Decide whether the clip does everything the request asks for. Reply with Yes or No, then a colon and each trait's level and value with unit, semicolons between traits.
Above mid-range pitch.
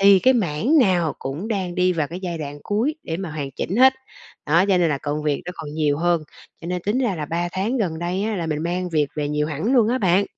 No: medium, 175 Hz